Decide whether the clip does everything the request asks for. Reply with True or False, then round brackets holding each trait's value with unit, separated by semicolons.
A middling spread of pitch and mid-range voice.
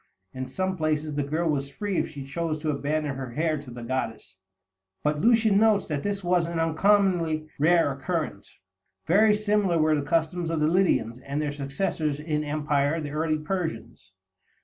True (3.6 semitones; 155 Hz)